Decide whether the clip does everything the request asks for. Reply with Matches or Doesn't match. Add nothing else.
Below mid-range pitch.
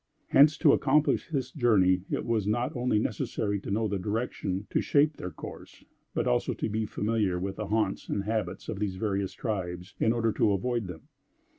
Matches